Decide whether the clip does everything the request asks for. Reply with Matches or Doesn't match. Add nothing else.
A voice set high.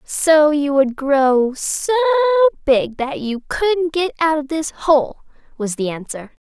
Matches